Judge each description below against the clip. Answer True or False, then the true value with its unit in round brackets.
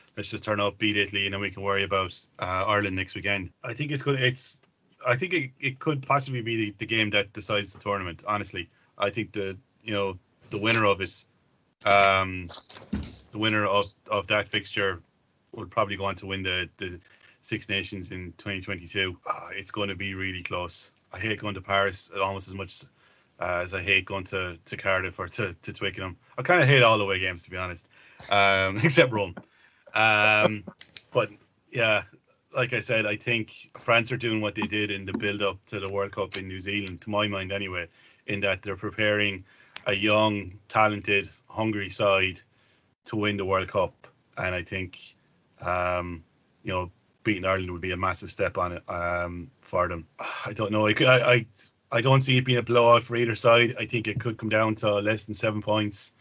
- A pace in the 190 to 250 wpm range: True (205 wpm)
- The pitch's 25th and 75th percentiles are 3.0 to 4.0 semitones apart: False (2.4 semitones)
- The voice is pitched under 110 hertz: True (100 Hz)